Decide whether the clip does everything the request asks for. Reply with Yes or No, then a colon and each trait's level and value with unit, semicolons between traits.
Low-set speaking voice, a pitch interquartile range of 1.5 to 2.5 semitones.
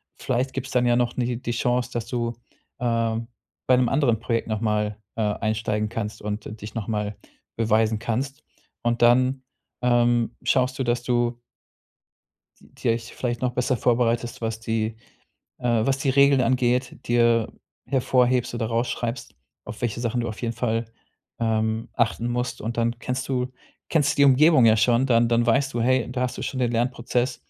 Yes: low, 120 Hz; narrow, 1.8 semitones